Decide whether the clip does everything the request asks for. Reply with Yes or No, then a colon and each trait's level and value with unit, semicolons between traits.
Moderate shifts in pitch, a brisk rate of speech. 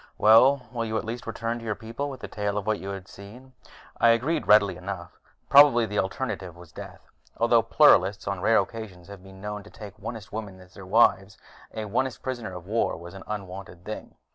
Yes: average, 3.1 semitones; fast, 210 wpm